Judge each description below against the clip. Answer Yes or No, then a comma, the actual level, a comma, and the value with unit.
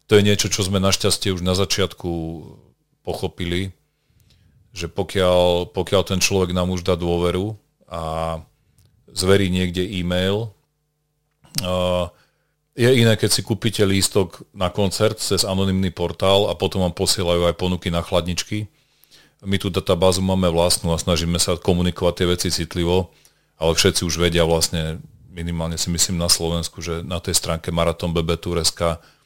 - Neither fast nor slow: Yes, average, 145 wpm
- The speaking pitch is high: No, very low, 90 Hz